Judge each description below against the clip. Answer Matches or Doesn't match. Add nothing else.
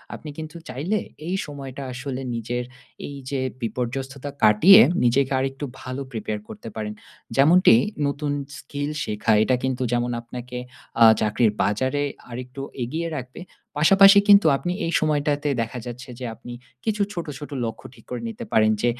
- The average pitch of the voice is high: Doesn't match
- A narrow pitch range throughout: Doesn't match